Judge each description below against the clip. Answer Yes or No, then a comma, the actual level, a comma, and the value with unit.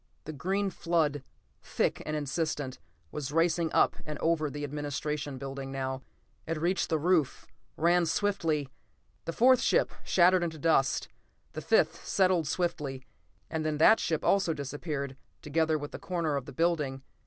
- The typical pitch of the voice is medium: Yes, medium, 155 Hz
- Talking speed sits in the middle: Yes, average, 155 wpm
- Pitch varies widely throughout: No, average, 2.9 semitones